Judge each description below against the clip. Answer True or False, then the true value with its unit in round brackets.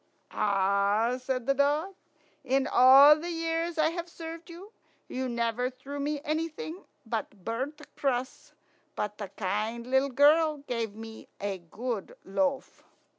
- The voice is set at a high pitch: True (260 Hz)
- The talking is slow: True (130 wpm)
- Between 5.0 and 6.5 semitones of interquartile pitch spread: True (5.3 semitones)